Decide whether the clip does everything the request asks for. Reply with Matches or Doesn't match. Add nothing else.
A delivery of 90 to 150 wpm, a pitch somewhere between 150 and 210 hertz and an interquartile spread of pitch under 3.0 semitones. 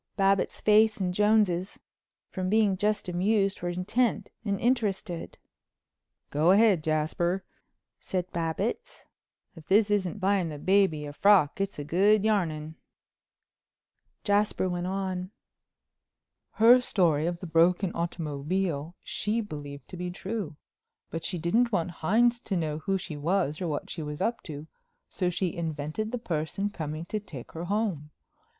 Doesn't match